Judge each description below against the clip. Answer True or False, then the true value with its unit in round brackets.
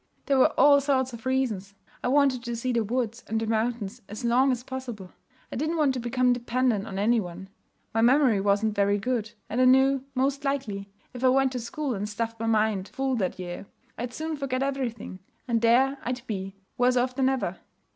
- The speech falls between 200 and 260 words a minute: True (205 wpm)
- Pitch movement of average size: True (3.4 semitones)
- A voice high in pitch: True (245 Hz)